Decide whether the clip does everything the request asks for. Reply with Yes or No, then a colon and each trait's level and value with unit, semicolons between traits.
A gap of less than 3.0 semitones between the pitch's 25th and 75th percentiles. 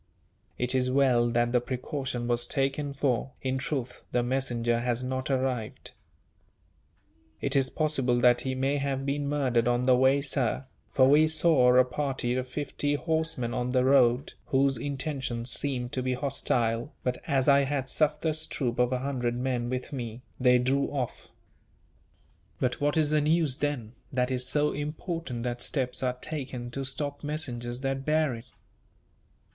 Yes: narrow, 2.4 semitones